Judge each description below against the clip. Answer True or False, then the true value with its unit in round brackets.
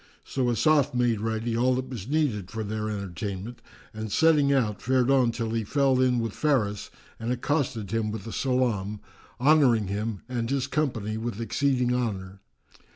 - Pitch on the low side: True (115 Hz)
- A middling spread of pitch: True (3.3 semitones)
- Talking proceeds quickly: False (165 wpm)